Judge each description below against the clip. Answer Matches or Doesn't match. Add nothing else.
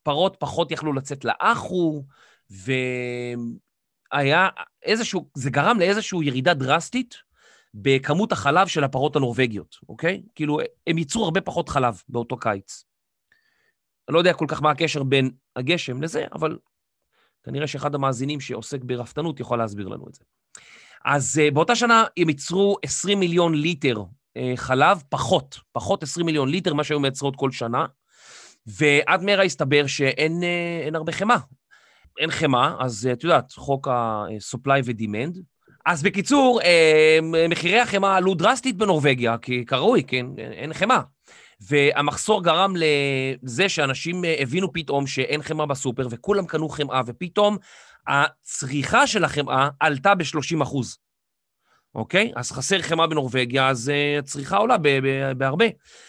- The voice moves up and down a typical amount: Matches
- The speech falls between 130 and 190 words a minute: Matches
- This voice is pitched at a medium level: Matches